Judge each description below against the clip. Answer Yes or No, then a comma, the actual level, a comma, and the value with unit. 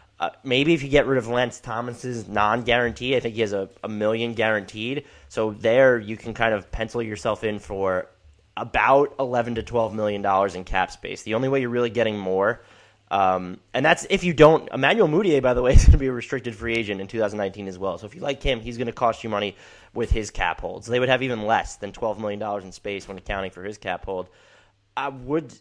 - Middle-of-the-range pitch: No, low, 115 Hz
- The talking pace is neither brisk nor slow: No, fast, 235 wpm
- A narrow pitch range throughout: No, average, 3.6 semitones